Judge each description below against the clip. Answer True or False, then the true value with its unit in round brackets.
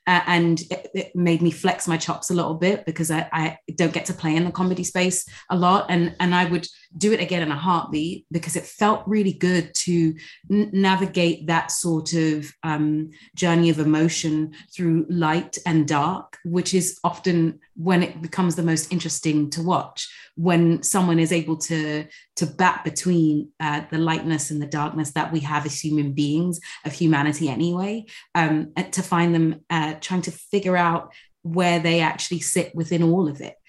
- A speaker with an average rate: True (185 wpm)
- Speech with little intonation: True (2.2 semitones)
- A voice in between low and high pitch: True (170 Hz)